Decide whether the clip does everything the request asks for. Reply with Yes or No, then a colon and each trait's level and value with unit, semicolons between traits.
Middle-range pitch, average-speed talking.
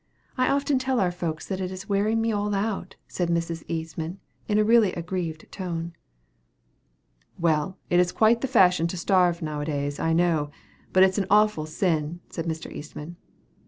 Yes: medium, 180 Hz; average, 185 wpm